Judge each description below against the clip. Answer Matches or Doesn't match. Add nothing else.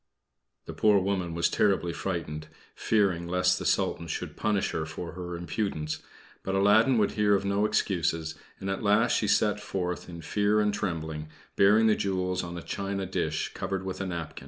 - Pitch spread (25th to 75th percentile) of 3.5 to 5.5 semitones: Doesn't match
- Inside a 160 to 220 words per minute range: Matches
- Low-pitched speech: Matches